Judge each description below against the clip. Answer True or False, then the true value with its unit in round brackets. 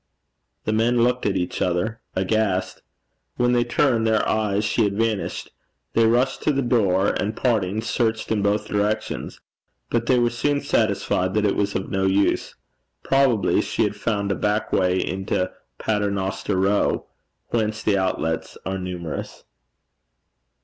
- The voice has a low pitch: True (105 Hz)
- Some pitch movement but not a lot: True (3.1 semitones)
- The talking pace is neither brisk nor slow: True (150 wpm)